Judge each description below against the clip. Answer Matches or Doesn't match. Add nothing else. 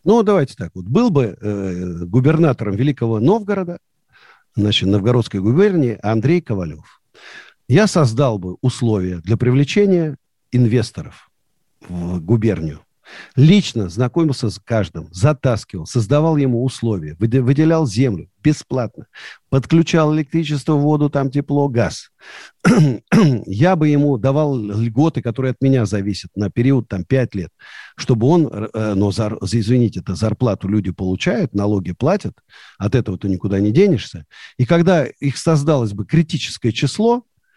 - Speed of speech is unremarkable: Matches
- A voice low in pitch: Matches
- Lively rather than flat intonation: Matches